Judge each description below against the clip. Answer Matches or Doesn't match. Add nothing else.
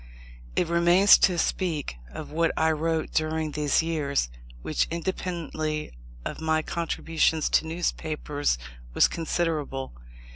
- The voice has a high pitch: Doesn't match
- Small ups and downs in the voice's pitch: Matches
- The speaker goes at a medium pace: Doesn't match